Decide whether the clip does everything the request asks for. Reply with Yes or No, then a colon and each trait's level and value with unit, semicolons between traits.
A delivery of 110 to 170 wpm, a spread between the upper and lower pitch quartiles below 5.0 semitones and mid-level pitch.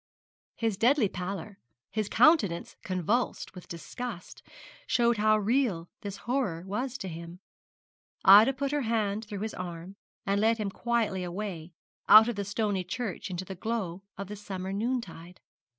No: average, 150 wpm; average, 3.8 semitones; high, 205 Hz